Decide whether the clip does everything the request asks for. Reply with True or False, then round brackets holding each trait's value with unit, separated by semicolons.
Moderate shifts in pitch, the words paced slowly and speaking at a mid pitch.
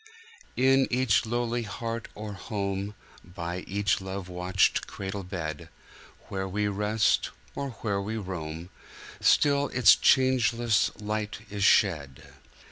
False (3.5 semitones; 115 wpm; 105 Hz)